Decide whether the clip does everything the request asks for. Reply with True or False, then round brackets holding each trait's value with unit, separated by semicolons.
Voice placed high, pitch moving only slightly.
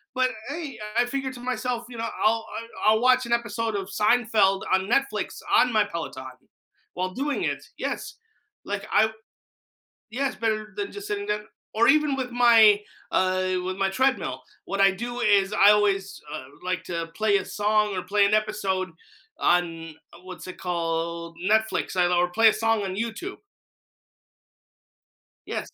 False (215 Hz; 4.2 semitones)